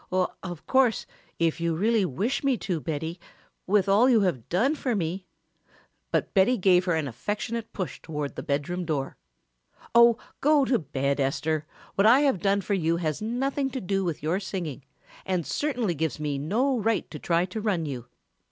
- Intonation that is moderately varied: No, wide, 6.2 semitones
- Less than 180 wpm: No, average, 185 wpm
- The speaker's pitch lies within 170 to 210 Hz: Yes, medium, 185 Hz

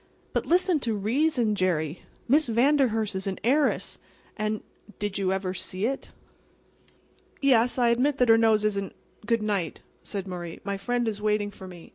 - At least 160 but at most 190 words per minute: Yes, average, 165 wpm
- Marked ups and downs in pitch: No, average, 3.9 semitones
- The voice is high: Yes, high, 215 Hz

